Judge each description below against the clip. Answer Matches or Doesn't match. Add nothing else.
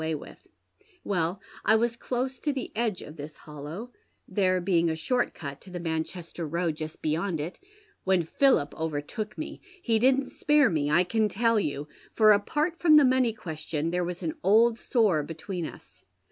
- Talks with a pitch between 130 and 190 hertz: Matches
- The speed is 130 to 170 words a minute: Doesn't match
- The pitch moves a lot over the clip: Matches